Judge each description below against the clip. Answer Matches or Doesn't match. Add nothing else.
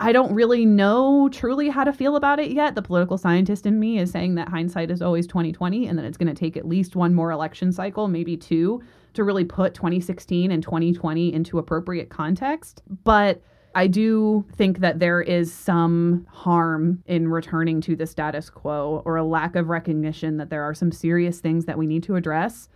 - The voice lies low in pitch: Doesn't match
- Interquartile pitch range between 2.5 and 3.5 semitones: Matches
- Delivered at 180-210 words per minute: Matches